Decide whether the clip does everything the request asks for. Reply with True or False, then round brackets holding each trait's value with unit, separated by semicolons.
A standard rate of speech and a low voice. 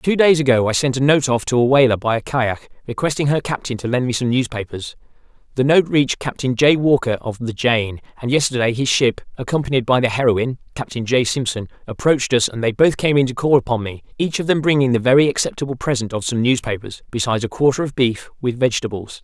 False (220 wpm; 125 Hz)